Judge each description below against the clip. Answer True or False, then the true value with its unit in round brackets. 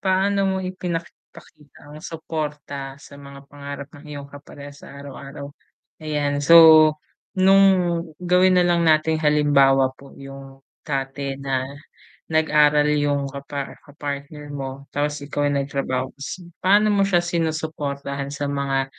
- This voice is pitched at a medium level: True (145 Hz)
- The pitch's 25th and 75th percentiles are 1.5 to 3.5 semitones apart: True (2.5 semitones)